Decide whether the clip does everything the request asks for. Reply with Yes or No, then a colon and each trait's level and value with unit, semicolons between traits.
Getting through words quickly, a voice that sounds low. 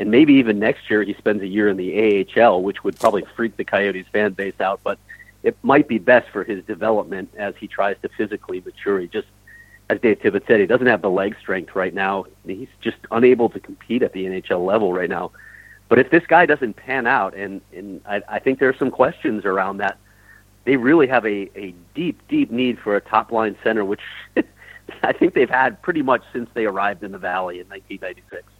Yes: fast, 220 wpm; low, 115 Hz